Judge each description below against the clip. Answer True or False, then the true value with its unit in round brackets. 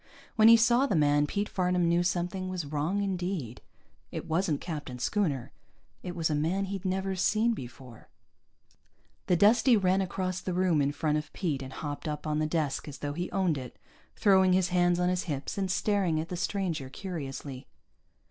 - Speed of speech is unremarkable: True (185 wpm)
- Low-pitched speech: False (175 Hz)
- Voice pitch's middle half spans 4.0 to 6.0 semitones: True (4.3 semitones)